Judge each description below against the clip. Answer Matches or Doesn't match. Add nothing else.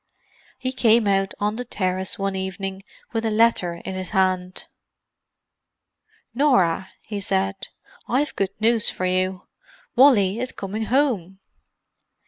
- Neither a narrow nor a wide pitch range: Matches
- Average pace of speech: Doesn't match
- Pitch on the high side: Matches